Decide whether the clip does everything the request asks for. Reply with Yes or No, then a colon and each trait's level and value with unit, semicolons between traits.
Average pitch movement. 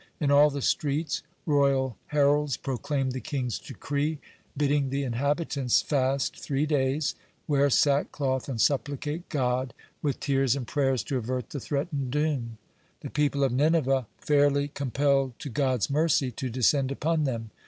No: narrow, 2.0 semitones